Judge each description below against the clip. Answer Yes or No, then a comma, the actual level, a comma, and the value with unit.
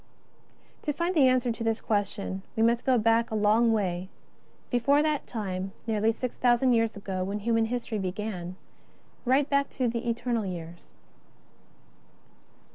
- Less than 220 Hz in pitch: No, high, 225 Hz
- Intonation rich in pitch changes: No, average, 3.3 semitones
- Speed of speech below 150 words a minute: No, average, 160 wpm